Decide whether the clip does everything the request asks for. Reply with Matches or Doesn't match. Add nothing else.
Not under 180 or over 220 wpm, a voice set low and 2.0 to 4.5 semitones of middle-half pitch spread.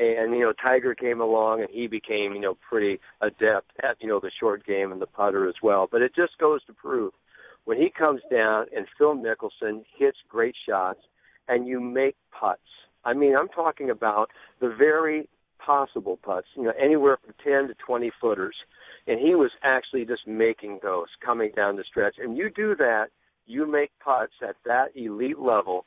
Doesn't match